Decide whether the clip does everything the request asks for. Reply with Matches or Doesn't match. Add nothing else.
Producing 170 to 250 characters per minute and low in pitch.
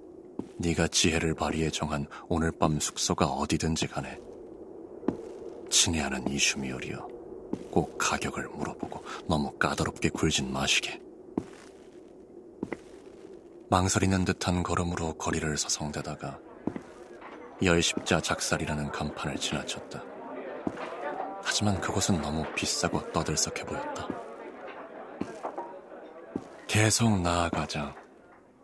Matches